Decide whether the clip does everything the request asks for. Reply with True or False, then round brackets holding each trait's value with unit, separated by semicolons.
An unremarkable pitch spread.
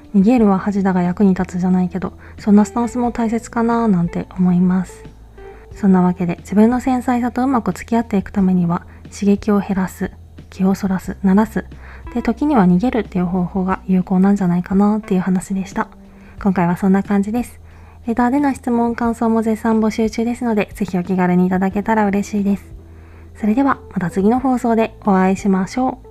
True (3.5 semitones)